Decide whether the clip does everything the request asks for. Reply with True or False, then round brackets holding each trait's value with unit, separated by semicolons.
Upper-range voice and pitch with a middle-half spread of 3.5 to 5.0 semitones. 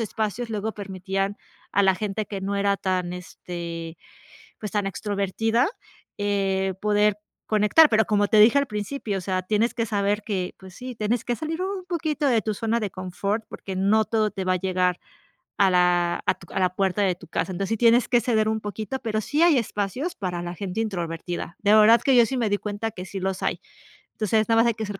False (205 Hz; 2.9 semitones)